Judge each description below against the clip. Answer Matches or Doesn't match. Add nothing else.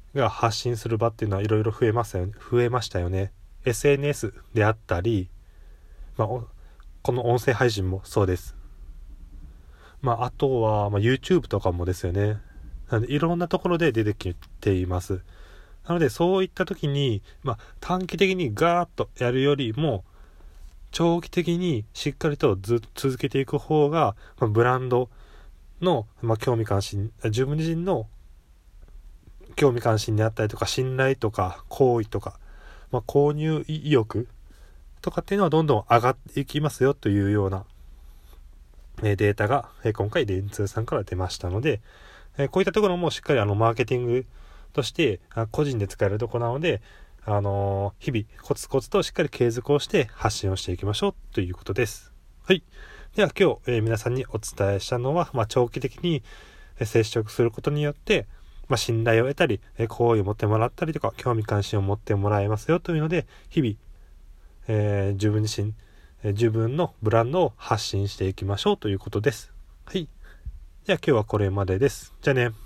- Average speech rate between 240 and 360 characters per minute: Matches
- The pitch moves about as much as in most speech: Doesn't match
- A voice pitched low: Matches